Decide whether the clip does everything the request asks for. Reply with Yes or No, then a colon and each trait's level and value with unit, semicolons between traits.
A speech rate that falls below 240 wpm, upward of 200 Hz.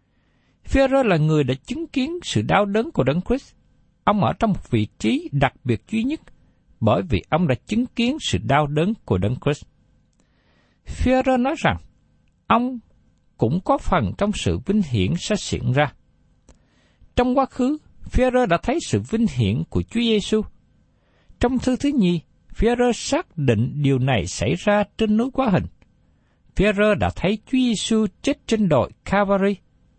Yes: average, 170 wpm; high, 210 Hz